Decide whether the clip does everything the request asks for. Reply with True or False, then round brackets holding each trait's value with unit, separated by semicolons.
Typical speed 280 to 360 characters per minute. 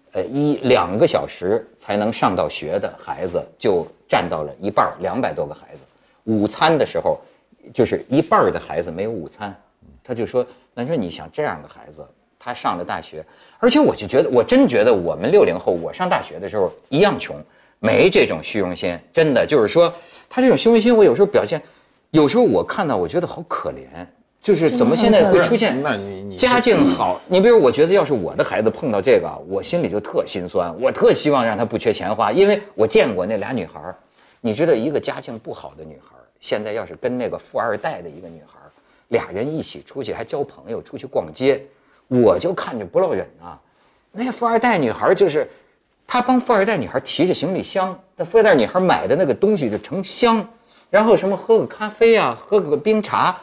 True (305 characters per minute)